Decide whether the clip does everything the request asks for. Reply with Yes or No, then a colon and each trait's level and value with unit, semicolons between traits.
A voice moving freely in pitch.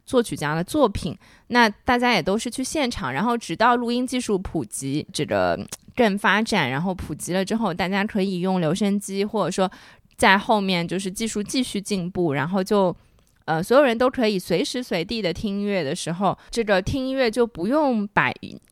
No: average, 4.9 semitones